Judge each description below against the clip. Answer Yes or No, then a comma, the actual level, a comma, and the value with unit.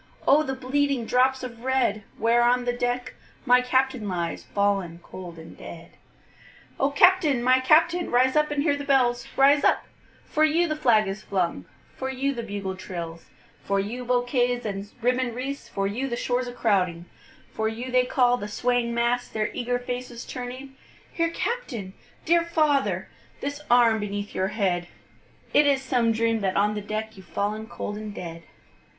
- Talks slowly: No, average, 175 wpm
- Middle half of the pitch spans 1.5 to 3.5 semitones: No, average, 4.2 semitones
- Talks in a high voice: Yes, high, 245 Hz